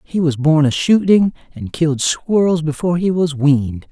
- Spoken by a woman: No, male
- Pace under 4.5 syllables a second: No, 5.0 syllables/s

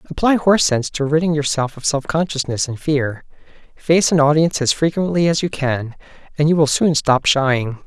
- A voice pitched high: No, medium, 150 Hz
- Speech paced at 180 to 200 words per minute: Yes, average, 190 wpm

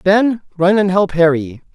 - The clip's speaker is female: No, male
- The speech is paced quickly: No, average, 170 wpm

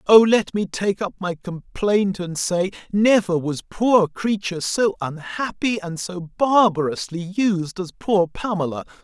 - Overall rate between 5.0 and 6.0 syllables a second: No, 4.0 syllables/s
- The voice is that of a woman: No, male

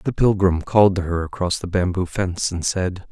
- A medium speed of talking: No, fast, 210 wpm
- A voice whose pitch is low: Yes, very low, 90 Hz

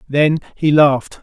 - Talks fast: No, average, 145 wpm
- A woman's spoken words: No, male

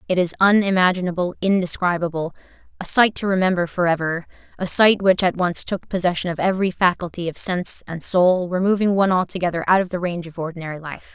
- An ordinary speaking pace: Yes, average, 180 wpm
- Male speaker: No, female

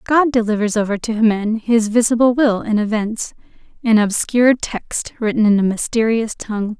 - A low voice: No, high, 225 Hz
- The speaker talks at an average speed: Yes, average, 160 wpm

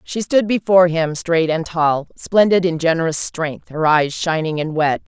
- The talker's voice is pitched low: No, medium, 165 Hz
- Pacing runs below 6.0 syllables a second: Yes, 4.5 syllables/s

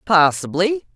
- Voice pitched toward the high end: Yes, high, 195 Hz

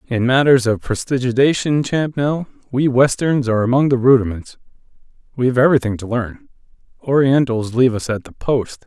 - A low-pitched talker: Yes, low, 125 Hz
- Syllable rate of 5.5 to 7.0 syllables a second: Yes, 5.6 syllables/s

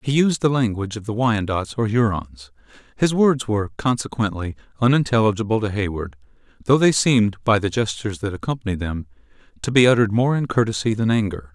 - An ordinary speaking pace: Yes, average, 170 wpm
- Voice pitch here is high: No, low, 110 Hz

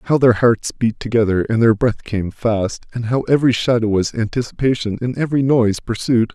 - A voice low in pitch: Yes, low, 115 Hz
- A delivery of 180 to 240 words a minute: Yes, average, 190 wpm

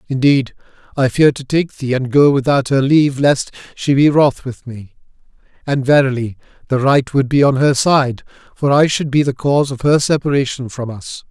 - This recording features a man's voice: Yes, male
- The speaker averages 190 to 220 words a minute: Yes, average, 195 wpm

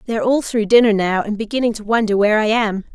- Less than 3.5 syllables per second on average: No, 6.7 syllables/s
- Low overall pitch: No, high, 220 Hz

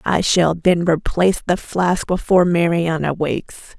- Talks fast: No, average, 145 wpm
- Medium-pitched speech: Yes, medium, 170 Hz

